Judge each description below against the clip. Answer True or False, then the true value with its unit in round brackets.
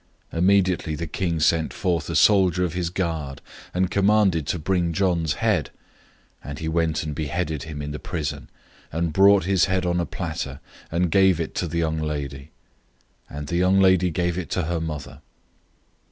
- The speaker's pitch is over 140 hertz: False (85 Hz)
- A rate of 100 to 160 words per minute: False (185 wpm)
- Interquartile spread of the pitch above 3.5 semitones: False (3.0 semitones)